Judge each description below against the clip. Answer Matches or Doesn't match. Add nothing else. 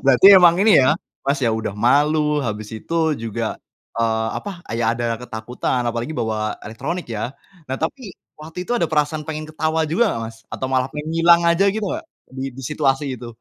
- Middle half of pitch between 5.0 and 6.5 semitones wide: Matches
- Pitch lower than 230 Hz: Matches